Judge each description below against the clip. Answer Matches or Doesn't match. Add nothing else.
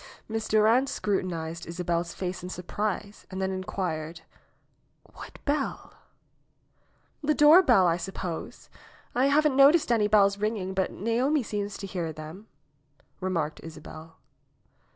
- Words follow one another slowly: Matches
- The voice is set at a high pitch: Matches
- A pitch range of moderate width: Matches